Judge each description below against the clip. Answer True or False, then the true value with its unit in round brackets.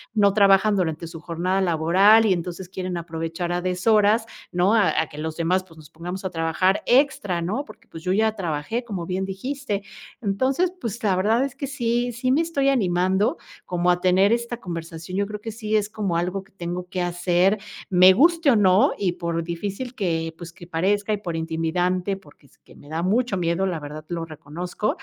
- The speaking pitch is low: False (185 Hz)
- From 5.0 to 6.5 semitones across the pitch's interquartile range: False (3.8 semitones)